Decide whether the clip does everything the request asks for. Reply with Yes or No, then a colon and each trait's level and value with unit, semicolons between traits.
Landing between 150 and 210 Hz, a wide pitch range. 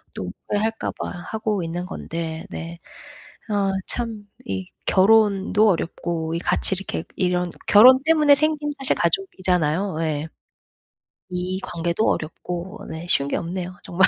No: medium, 185 Hz; average, 4.2 semitones